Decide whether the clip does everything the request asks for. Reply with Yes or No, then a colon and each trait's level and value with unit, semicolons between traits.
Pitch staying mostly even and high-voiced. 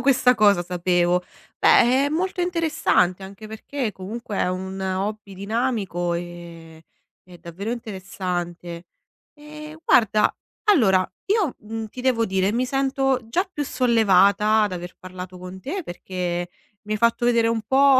No: wide, 5.6 semitones; high, 210 Hz